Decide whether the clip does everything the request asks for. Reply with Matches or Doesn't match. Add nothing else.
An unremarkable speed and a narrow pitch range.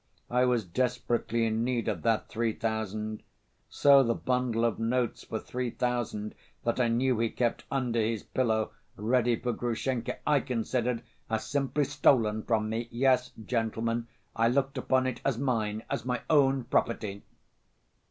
Matches